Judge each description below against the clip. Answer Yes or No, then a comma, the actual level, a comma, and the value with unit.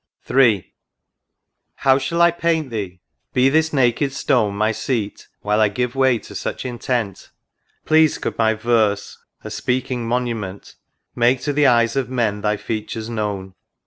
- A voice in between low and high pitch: No, low, 120 Hz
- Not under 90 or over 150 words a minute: No, average, 170 wpm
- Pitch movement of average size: Yes, average, 3.8 semitones